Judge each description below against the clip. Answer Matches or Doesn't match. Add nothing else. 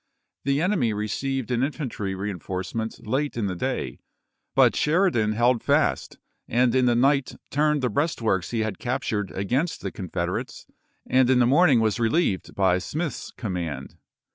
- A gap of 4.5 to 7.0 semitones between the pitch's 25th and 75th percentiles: Matches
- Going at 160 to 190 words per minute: Doesn't match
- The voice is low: Matches